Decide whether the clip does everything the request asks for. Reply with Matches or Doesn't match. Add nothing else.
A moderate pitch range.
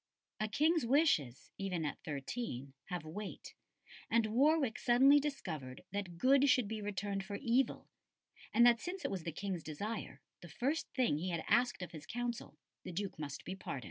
Doesn't match